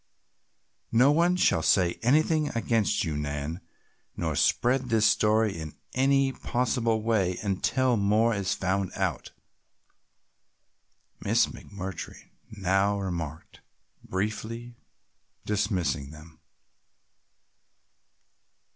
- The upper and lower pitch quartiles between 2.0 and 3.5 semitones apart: No, average, 4.5 semitones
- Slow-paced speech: Yes, slow, 90 wpm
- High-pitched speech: No, low, 105 Hz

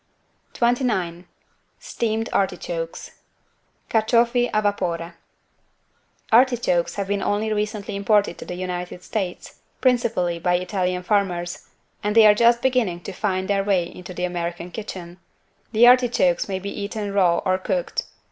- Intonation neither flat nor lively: Yes, average, 3.9 semitones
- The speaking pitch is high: Yes, high, 200 Hz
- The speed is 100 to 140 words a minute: Yes, slow, 135 wpm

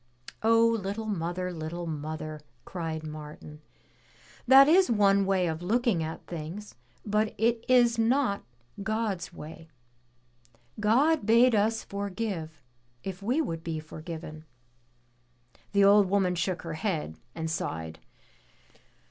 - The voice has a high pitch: Yes, high, 195 Hz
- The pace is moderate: No, slow, 120 wpm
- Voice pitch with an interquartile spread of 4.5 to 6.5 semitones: Yes, wide, 5.6 semitones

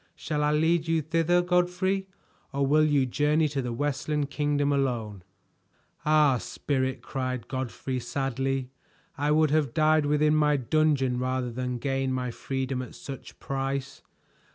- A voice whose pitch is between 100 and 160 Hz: Yes, medium, 140 Hz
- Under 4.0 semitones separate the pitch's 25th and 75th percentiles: Yes, average, 2.8 semitones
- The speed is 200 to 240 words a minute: No, average, 145 wpm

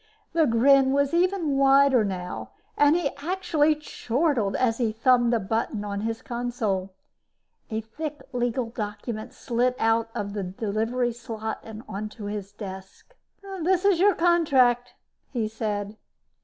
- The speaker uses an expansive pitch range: No, average, 4.6 semitones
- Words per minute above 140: No, slow, 135 wpm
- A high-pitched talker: Yes, high, 240 Hz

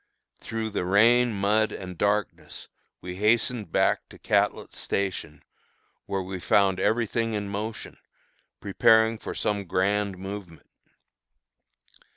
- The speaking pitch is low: Yes, low, 100 Hz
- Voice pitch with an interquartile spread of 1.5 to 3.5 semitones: Yes, average, 2.7 semitones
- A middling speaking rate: No, slow, 120 wpm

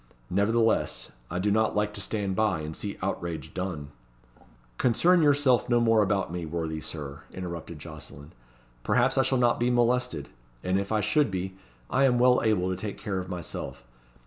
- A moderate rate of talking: Yes, average, 175 wpm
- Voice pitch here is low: Yes, low, 100 Hz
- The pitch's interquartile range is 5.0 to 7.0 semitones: Yes, wide, 5.6 semitones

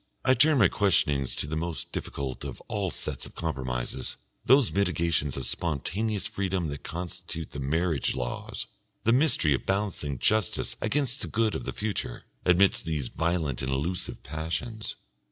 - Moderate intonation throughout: No, wide, 6.1 semitones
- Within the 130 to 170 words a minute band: Yes, average, 155 wpm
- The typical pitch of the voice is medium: No, very low, 85 Hz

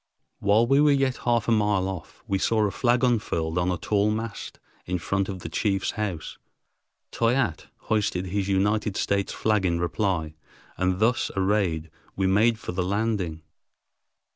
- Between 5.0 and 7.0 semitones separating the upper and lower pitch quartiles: No, average, 3.3 semitones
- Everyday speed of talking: Yes, average, 165 wpm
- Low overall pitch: Yes, low, 100 Hz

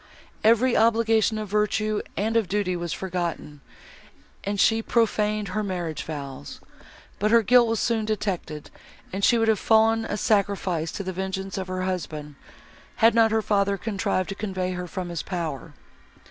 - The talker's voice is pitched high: Yes, high, 200 Hz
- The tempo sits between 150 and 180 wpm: Yes, average, 165 wpm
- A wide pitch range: No, average, 3.3 semitones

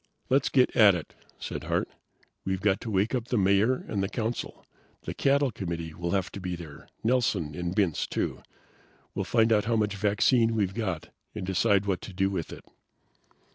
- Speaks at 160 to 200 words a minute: Yes, average, 190 wpm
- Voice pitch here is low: Yes, low, 100 Hz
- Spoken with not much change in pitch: No, average, 3.6 semitones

